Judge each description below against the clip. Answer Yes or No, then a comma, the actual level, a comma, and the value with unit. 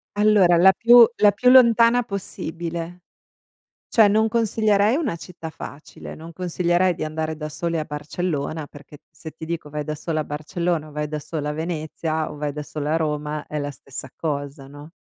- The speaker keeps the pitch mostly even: No, average, 3.7 semitones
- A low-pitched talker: No, medium, 160 Hz